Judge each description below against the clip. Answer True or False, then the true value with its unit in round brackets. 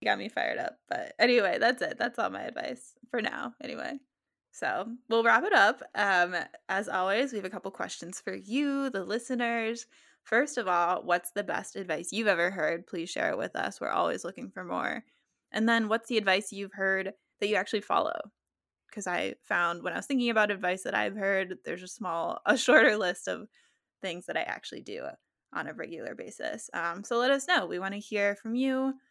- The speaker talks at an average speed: False (210 wpm)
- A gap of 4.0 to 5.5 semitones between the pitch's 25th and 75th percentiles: True (4.6 semitones)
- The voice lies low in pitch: False (210 Hz)